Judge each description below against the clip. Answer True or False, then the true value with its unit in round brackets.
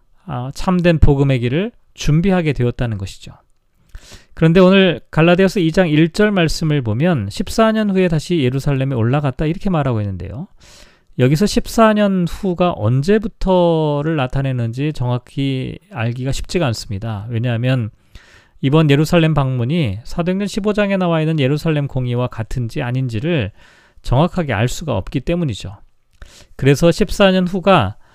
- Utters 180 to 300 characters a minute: False (310 characters per minute)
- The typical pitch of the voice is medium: True (145 Hz)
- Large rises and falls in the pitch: True (6.4 semitones)